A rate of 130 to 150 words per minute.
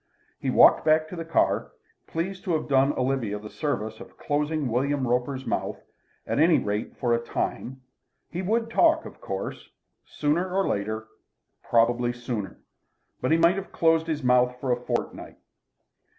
No: average, 165 wpm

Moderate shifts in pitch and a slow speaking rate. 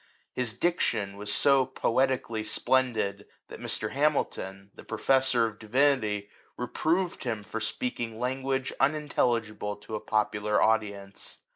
Yes: average, 4.1 semitones; slow, 125 wpm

